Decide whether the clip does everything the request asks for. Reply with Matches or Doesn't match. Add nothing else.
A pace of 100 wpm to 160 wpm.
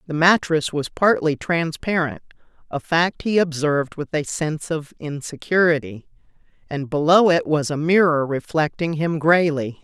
Matches